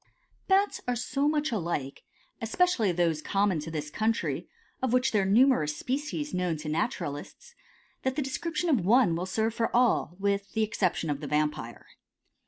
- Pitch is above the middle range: Yes, high, 210 Hz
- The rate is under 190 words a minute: Yes, average, 170 wpm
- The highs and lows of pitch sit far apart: Yes, wide, 7.8 semitones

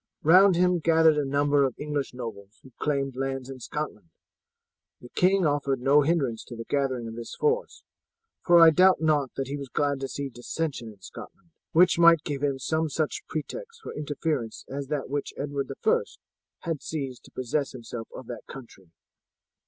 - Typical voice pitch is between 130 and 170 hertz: Yes, medium, 140 Hz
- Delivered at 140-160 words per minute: No, average, 185 wpm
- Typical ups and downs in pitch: Yes, average, 3.7 semitones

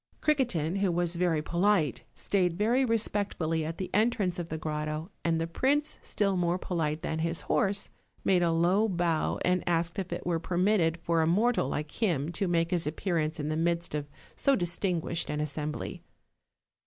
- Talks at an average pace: Yes, average, 180 wpm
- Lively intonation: No, average, 3.2 semitones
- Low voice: No, medium, 170 Hz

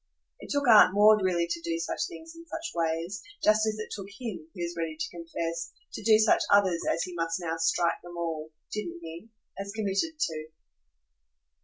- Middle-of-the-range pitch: Yes, medium, 175 Hz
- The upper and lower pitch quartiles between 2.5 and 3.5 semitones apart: No, average, 4.3 semitones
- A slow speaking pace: No, average, 195 wpm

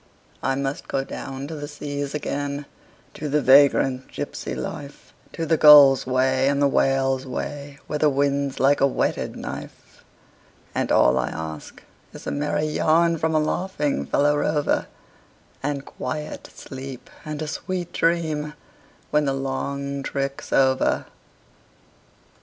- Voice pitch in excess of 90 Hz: Yes, medium, 140 Hz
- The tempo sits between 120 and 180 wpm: Yes, average, 140 wpm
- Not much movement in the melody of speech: Yes, narrow, 1.9 semitones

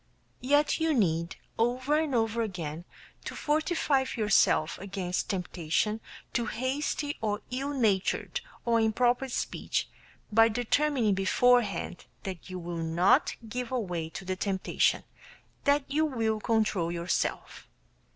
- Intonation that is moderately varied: No, wide, 5.7 semitones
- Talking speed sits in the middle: No, slow, 120 wpm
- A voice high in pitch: Yes, high, 225 Hz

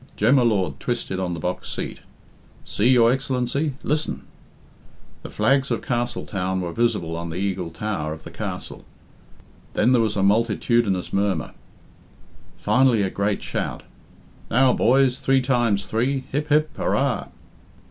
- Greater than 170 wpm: No, average, 145 wpm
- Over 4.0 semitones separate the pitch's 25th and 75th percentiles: Yes, wide, 5.6 semitones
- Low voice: Yes, low, 115 Hz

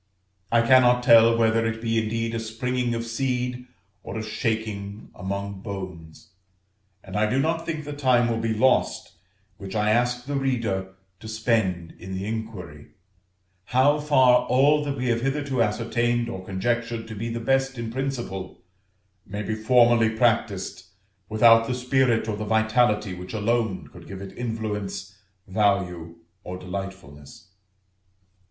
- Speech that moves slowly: No, average, 150 wpm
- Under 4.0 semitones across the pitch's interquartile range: Yes, average, 3.5 semitones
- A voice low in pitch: Yes, low, 115 Hz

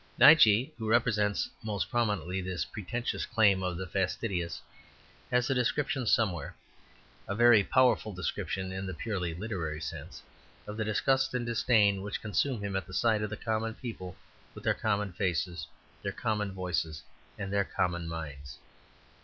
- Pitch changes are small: No, average, 3.6 semitones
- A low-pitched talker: Yes, low, 100 Hz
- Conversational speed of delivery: Yes, average, 155 wpm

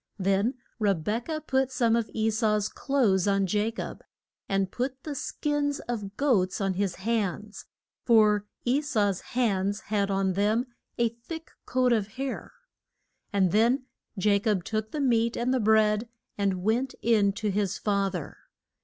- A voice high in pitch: Yes, high, 215 Hz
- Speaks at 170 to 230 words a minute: No, average, 160 wpm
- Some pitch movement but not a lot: Yes, average, 3.4 semitones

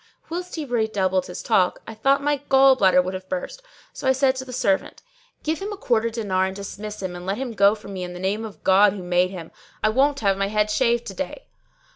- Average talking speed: No, fast, 245 wpm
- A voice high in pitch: Yes, high, 210 Hz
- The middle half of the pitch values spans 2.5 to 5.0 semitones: No, wide, 5.6 semitones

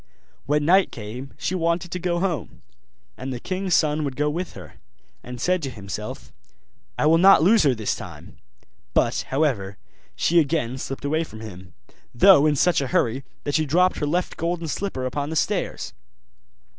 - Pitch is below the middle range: No, medium, 150 Hz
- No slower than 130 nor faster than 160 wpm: No, average, 180 wpm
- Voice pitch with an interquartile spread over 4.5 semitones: Yes, average, 5.2 semitones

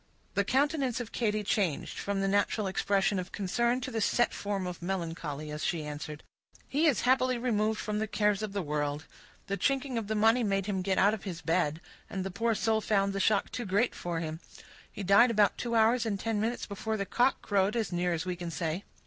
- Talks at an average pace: No, fast, 225 wpm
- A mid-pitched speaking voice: No, high, 200 Hz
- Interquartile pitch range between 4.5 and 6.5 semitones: No, average, 3.8 semitones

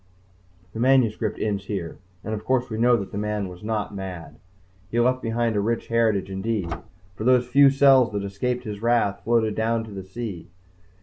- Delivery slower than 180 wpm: No, average, 195 wpm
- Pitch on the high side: No, low, 110 Hz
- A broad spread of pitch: No, average, 3.0 semitones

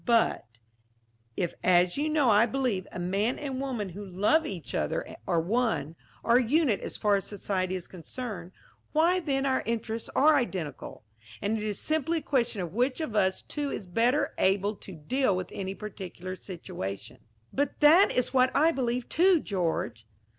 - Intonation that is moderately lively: No, wide, 6.5 semitones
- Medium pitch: No, high, 220 Hz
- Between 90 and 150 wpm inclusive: No, average, 175 wpm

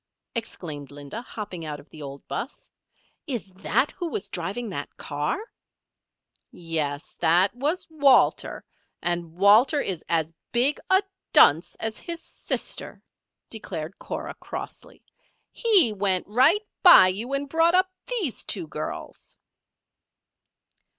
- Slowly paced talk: Yes, slow, 125 wpm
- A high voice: Yes, high, 205 Hz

